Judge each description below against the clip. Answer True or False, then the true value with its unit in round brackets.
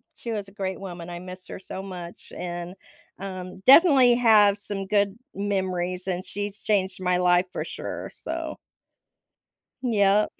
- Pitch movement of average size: False (2.1 semitones)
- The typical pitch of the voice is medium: False (195 Hz)